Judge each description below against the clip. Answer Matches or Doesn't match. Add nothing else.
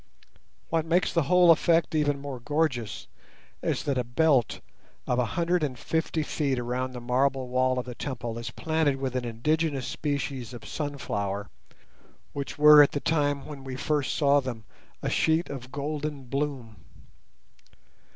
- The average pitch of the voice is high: Doesn't match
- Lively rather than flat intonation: Doesn't match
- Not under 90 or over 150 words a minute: Doesn't match